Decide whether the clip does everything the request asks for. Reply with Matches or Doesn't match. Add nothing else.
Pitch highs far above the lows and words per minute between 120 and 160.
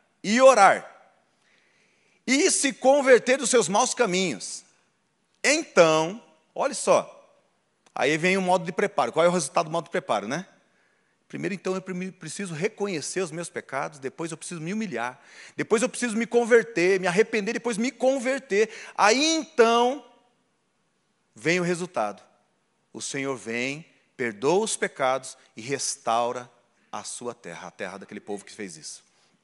Matches